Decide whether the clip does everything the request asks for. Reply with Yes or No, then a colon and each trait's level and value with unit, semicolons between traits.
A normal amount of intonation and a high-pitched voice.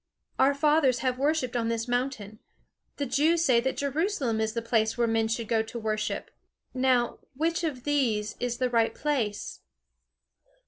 Yes: average, 3.9 semitones; high, 245 Hz